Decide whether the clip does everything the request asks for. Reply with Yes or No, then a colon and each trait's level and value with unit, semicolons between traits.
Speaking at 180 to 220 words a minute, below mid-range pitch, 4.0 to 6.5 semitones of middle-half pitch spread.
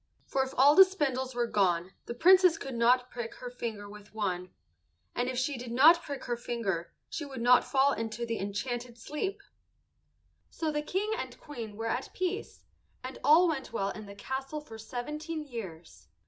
No: average, 185 wpm; very high, 250 Hz; average, 4.9 semitones